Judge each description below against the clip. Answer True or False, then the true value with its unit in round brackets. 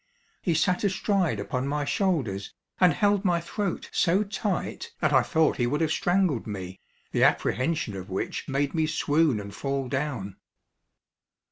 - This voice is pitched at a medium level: True (150 Hz)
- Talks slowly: False (155 wpm)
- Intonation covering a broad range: True (6.6 semitones)